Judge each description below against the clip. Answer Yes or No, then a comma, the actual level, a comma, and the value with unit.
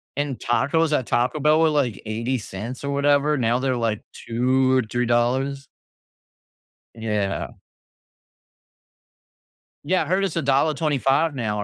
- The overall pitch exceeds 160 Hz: No, low, 130 Hz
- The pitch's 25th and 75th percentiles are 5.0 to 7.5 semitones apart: No, average, 3.6 semitones